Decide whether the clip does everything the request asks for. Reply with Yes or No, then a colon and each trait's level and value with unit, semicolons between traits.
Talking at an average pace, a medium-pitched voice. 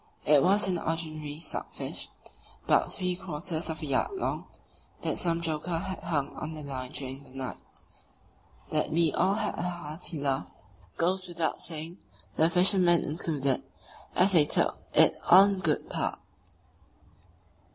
Yes: average, 150 wpm; medium, 165 Hz